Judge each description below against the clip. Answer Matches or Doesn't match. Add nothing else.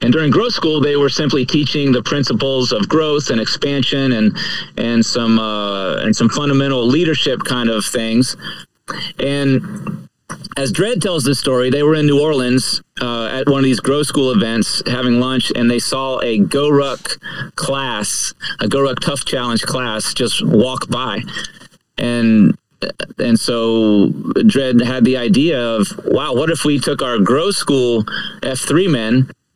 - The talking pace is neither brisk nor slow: Matches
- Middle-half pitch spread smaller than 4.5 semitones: Matches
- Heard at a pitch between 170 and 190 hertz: Doesn't match